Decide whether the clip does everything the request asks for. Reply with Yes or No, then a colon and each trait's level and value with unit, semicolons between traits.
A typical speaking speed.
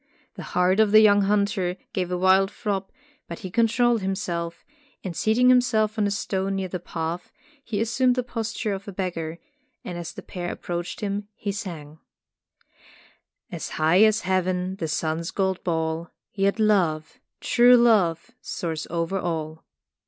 Yes: average, 160 wpm